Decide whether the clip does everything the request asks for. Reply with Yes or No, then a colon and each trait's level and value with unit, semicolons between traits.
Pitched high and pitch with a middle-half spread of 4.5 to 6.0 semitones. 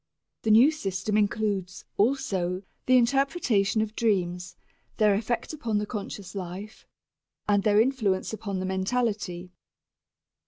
No: high, 210 Hz; average, 3.4 semitones